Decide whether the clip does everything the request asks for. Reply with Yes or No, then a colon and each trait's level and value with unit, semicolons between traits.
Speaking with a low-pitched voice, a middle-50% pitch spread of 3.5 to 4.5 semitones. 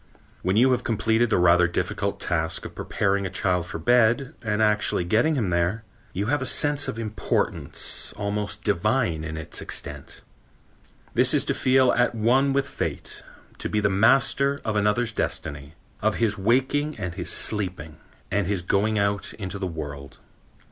No: low, 105 Hz; average, 5.0 semitones